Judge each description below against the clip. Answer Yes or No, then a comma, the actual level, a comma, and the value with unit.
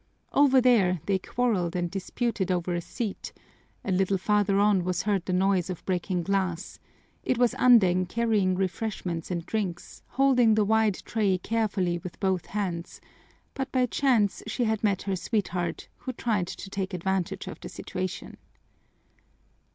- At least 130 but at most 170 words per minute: Yes, average, 155 wpm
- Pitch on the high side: Yes, high, 195 Hz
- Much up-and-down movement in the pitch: No, average, 3.4 semitones